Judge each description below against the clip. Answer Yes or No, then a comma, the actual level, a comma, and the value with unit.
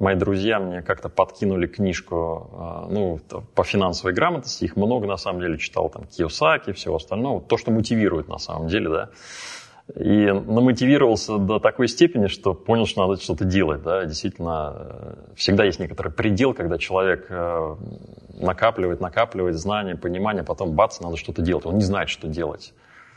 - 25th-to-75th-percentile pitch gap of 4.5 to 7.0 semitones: No, average, 3.3 semitones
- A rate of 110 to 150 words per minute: No, fast, 160 wpm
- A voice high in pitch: No, very low, 95 Hz